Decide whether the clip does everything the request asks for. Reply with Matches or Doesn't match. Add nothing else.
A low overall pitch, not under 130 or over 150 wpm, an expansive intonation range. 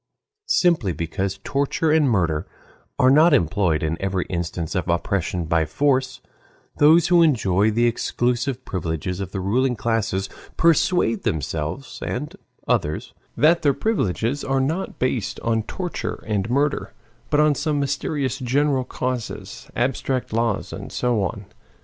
Matches